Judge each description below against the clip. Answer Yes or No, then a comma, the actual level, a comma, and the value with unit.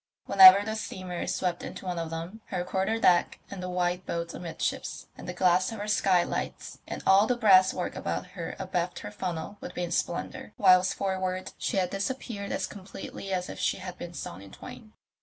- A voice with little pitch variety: Yes, narrow, 1.8 semitones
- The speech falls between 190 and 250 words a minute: Yes, average, 200 wpm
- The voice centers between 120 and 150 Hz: No, medium, 185 Hz